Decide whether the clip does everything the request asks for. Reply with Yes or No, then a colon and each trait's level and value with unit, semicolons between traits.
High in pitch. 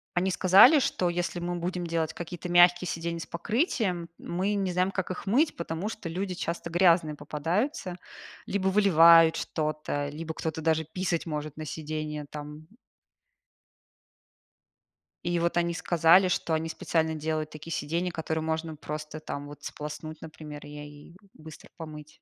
No: medium, 165 Hz